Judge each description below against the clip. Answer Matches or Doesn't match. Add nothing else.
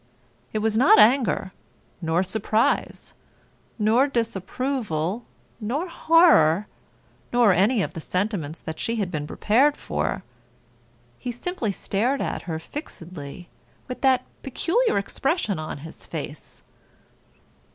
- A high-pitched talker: Matches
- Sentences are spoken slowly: Matches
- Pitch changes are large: Matches